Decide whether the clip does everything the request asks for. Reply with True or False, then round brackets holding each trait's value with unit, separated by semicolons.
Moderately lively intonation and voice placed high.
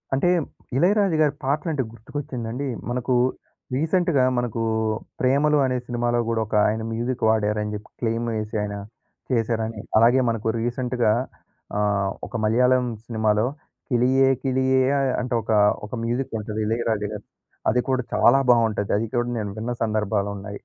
False (3.1 semitones; 120 Hz)